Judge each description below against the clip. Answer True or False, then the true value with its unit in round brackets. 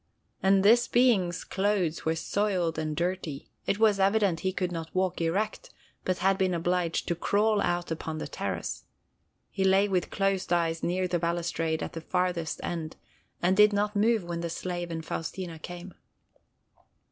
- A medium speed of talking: True (170 wpm)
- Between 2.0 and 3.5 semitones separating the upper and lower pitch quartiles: True (2.7 semitones)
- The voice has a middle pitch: True (180 Hz)